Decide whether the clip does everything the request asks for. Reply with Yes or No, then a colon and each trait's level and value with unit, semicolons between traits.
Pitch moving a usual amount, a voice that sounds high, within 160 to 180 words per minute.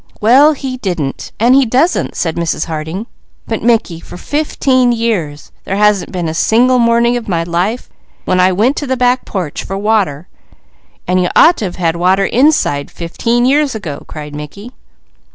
No: wide, 6.3 semitones; high, 210 Hz; average, 170 wpm